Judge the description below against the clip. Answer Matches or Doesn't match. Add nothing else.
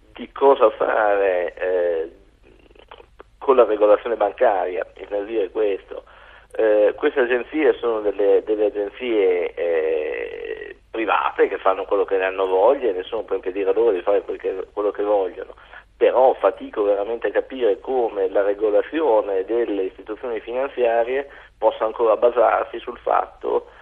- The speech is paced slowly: Doesn't match